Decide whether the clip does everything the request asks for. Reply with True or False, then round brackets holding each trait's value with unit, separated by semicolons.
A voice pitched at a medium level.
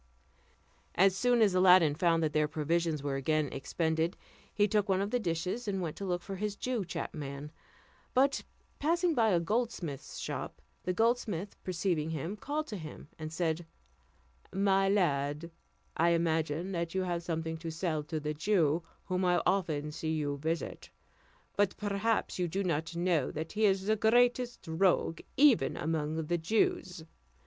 True (175 Hz)